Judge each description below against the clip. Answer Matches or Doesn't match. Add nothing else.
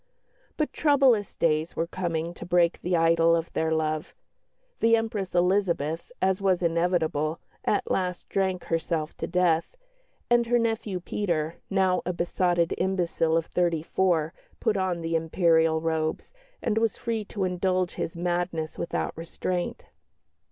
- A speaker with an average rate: Matches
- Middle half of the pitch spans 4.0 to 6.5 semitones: Doesn't match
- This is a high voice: Doesn't match